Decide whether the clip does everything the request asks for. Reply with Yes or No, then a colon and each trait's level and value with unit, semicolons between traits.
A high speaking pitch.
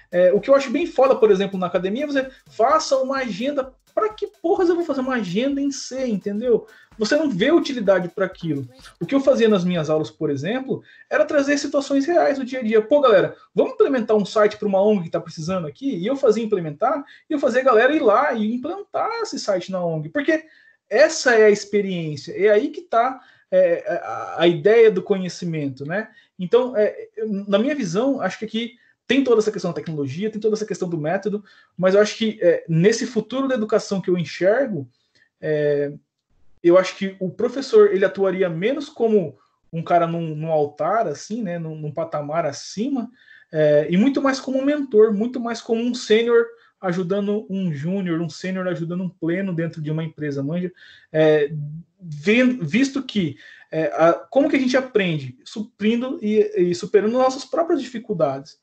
Yes: high, 210 Hz